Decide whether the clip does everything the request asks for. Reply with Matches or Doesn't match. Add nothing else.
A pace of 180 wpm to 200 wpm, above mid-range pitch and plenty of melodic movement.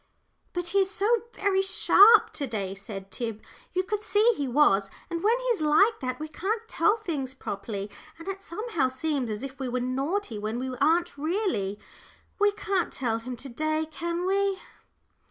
Matches